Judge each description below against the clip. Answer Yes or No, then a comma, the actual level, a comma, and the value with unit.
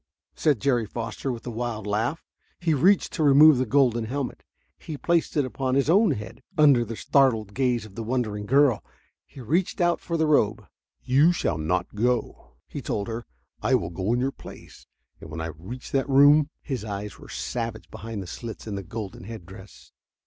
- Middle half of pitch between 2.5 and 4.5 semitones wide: No, average, 4.9 semitones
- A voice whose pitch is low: Yes, low, 120 Hz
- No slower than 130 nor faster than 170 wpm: No, average, 195 wpm